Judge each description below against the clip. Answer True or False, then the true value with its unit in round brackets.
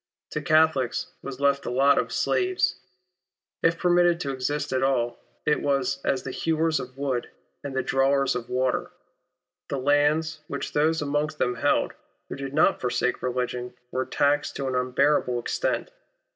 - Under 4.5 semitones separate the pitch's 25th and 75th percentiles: True (2.9 semitones)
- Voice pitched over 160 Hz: False (140 Hz)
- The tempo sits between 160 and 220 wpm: True (165 wpm)